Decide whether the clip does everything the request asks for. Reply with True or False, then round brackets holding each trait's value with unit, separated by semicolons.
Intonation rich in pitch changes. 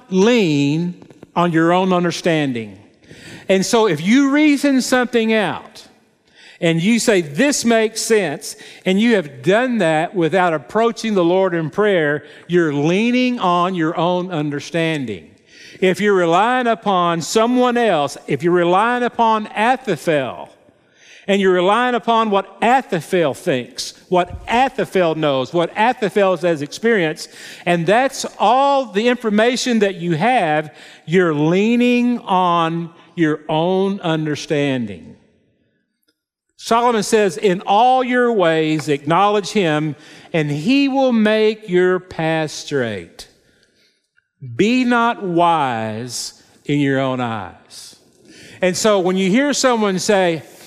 True (5.8 semitones)